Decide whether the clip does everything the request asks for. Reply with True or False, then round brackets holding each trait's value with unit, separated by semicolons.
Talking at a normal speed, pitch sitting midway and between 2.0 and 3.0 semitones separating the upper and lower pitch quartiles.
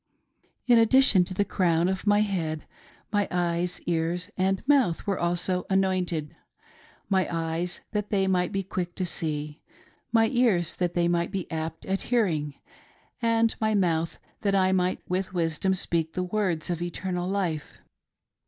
True (155 wpm; 180 Hz; 2.5 semitones)